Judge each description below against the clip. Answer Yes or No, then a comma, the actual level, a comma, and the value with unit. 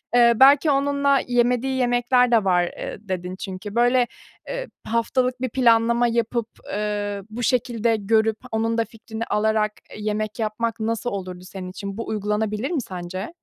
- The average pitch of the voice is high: Yes, high, 225 Hz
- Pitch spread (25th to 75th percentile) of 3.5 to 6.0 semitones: No, average, 2.7 semitones